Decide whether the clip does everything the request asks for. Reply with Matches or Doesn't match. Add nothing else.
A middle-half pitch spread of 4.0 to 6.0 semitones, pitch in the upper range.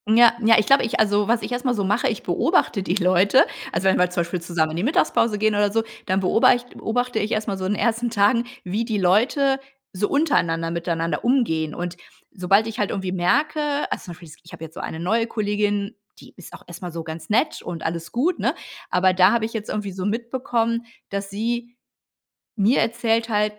Matches